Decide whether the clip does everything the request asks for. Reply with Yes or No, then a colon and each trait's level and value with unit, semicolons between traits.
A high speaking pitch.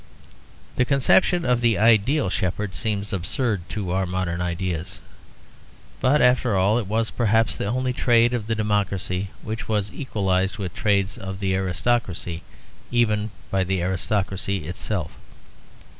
No: low, 100 Hz